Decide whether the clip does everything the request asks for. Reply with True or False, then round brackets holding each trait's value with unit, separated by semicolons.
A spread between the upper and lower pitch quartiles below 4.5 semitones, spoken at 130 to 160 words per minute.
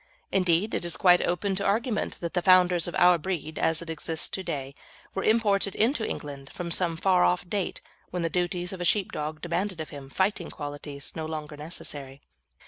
False (3.3 semitones; 195 wpm)